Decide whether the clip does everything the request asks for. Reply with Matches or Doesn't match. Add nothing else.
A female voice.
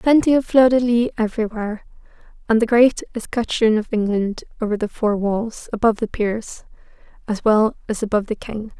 Matches